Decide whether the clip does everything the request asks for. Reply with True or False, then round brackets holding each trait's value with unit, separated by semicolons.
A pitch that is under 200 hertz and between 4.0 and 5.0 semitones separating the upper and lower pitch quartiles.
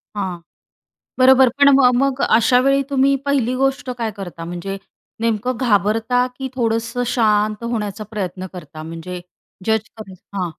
False (225 Hz; 4.6 semitones)